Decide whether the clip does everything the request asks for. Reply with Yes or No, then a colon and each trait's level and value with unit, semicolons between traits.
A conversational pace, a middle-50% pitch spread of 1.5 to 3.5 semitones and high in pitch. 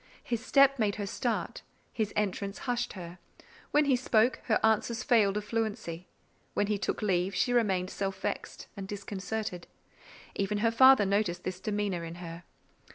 Yes: average, 160 wpm; average, 3.2 semitones; high, 205 Hz